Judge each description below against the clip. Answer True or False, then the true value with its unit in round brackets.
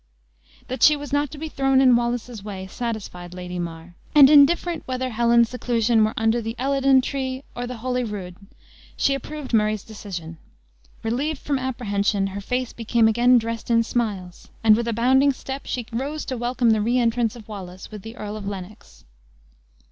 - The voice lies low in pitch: False (235 Hz)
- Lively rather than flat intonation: False (3.5 semitones)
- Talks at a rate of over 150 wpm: True (180 wpm)